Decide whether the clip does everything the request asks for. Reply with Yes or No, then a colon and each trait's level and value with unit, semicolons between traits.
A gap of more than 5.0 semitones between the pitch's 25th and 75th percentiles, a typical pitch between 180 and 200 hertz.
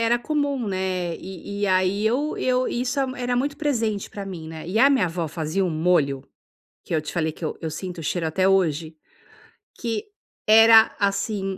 Yes: wide, 5.4 semitones; high, 195 Hz